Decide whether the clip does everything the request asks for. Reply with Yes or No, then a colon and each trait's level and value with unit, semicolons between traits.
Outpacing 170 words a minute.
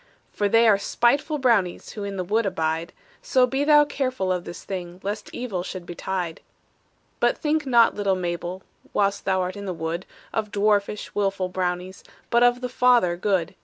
Yes: average, 180 wpm